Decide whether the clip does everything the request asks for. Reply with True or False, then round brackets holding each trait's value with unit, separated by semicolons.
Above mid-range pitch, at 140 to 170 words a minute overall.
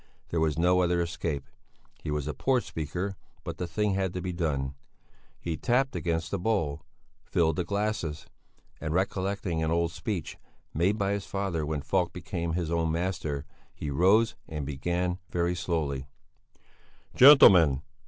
False (85 Hz; 155 wpm)